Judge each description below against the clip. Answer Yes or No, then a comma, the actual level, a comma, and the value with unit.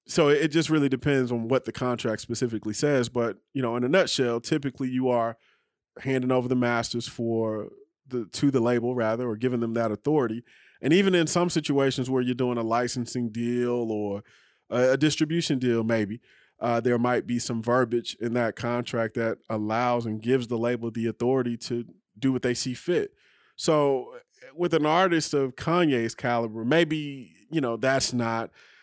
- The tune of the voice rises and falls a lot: No, average, 2.8 semitones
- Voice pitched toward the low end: Yes, low, 125 Hz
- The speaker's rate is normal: Yes, average, 180 wpm